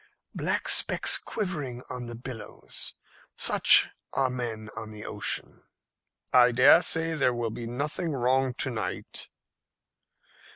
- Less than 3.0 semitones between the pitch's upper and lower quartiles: Yes, narrow, 2.5 semitones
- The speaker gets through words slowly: Yes, slow, 125 wpm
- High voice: No, low, 125 Hz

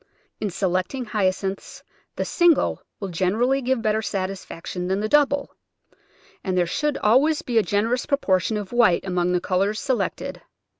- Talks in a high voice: Yes, high, 210 Hz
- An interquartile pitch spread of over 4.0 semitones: Yes, average, 5.2 semitones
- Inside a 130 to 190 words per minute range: Yes, average, 160 wpm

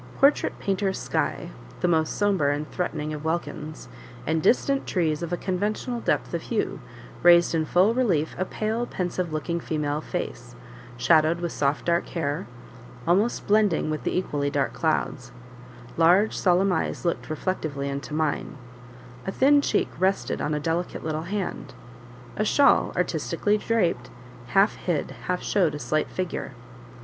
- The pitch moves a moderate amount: Yes, average, 4.1 semitones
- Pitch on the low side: No, medium, 170 Hz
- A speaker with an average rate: Yes, average, 155 wpm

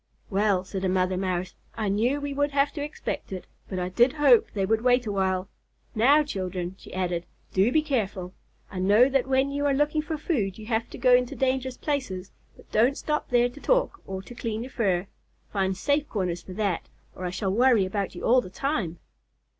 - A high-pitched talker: Yes, high, 220 Hz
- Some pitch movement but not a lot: No, wide, 6.2 semitones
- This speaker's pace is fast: Yes, fast, 215 wpm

